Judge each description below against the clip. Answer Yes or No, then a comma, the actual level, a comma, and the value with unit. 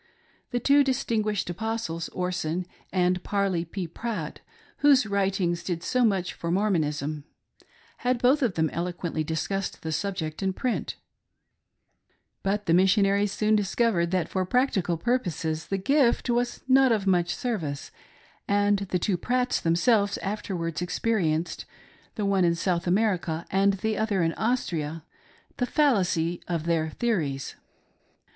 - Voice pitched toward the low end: No, high, 190 Hz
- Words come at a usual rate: Yes, average, 145 wpm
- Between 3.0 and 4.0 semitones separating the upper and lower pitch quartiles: No, average, 4.6 semitones